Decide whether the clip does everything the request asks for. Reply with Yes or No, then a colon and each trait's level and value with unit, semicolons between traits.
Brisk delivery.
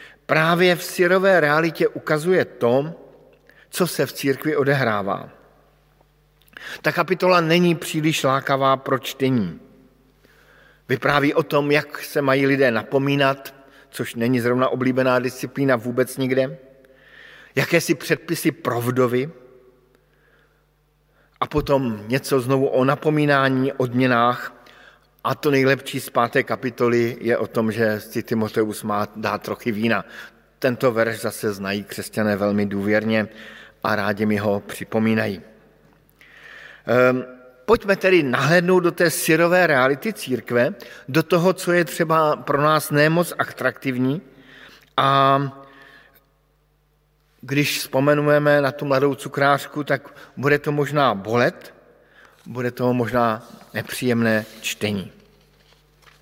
No: average, 115 wpm